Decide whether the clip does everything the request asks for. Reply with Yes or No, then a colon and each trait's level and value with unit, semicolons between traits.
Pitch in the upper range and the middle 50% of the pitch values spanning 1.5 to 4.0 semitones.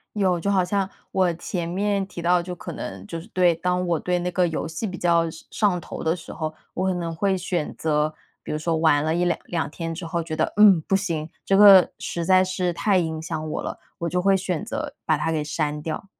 No: medium, 175 Hz; narrow, 2.5 semitones